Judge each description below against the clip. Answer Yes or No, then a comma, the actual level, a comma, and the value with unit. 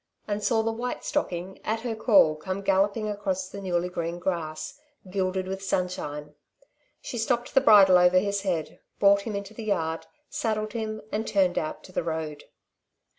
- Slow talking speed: No, average, 175 wpm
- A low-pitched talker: No, high, 195 Hz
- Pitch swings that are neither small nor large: Yes, average, 3.3 semitones